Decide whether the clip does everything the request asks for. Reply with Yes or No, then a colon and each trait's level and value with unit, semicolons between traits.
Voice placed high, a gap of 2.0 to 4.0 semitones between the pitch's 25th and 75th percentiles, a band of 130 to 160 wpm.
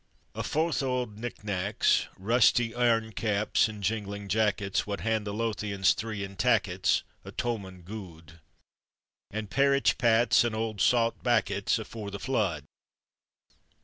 No: low, 110 Hz; narrow, 2.6 semitones; average, 140 wpm